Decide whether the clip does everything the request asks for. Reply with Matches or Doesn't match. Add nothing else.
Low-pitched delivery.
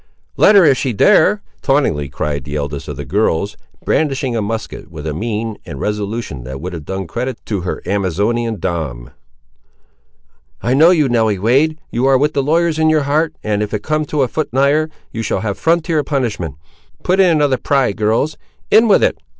Matches